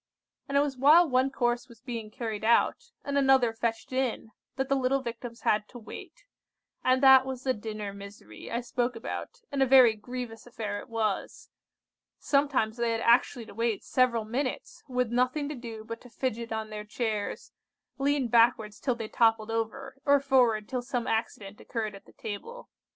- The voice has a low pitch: No, high, 240 Hz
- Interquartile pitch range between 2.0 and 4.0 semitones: Yes, average, 3.0 semitones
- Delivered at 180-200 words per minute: Yes, average, 185 wpm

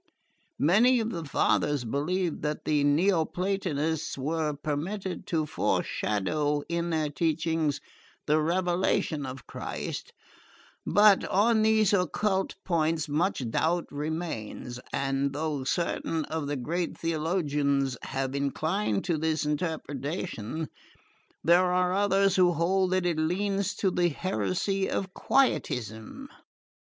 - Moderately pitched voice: Yes, medium, 160 Hz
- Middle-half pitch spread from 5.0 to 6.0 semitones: No, average, 4.2 semitones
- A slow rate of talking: Yes, slow, 115 wpm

